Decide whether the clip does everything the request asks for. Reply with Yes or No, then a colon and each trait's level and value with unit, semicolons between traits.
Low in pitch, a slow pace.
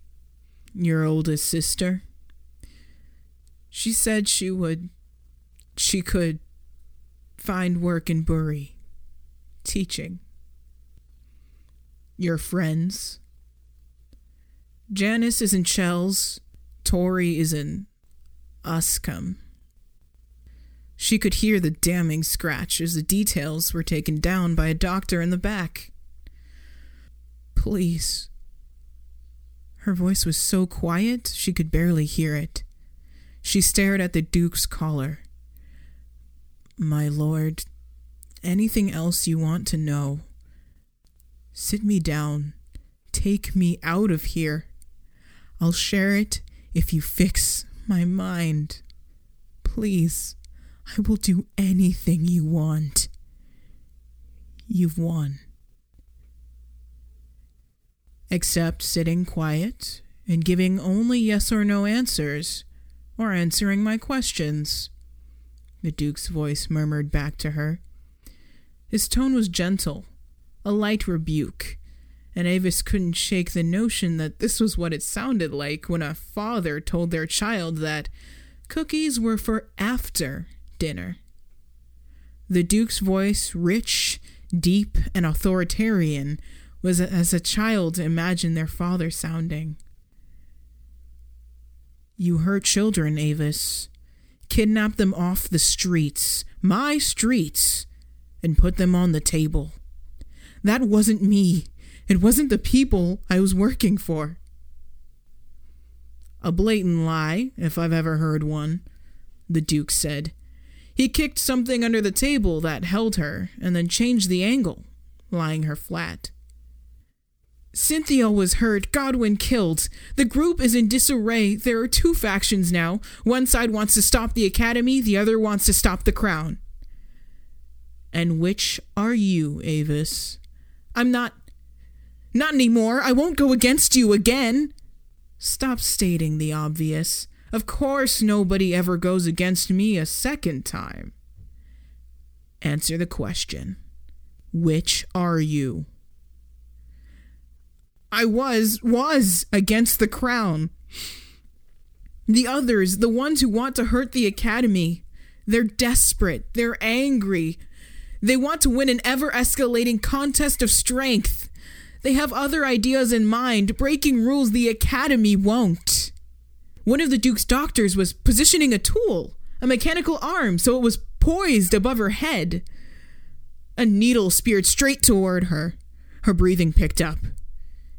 No: medium, 165 Hz; slow, 120 wpm